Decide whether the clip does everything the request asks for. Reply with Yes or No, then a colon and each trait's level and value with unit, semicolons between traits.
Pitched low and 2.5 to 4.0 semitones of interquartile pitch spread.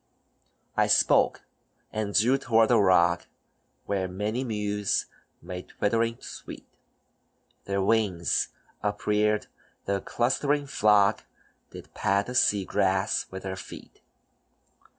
Yes: low, 105 Hz; average, 2.8 semitones